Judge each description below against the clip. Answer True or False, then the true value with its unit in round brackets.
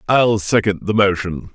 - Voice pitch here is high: False (100 Hz)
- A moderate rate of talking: True (155 wpm)